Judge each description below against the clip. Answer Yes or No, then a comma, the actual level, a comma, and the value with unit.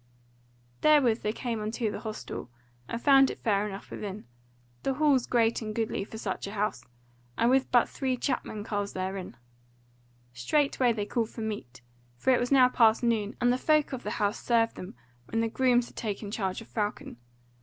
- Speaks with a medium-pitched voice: No, high, 225 Hz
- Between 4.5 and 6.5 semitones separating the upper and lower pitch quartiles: No, average, 3.2 semitones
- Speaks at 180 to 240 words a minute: Yes, average, 185 wpm